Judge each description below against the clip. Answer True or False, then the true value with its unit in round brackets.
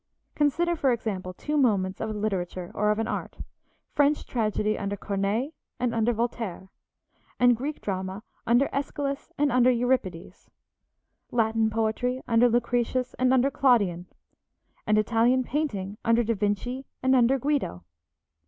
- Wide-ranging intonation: False (3.6 semitones)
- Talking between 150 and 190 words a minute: False (140 wpm)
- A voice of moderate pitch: False (230 Hz)